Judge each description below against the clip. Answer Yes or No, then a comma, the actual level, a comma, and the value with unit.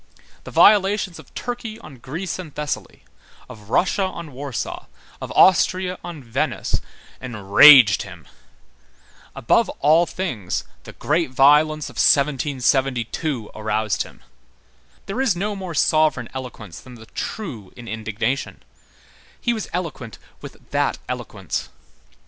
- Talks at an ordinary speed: No, slow, 120 wpm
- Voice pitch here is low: No, medium, 145 Hz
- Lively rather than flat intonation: Yes, wide, 7.0 semitones